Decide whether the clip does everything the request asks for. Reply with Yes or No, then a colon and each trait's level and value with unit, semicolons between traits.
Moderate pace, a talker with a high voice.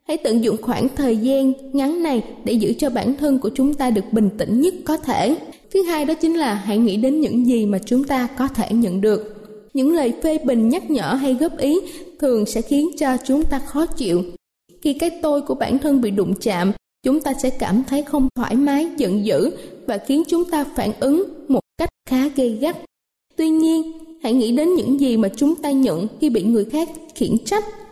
Yes: average, 220 wpm; very high, 270 Hz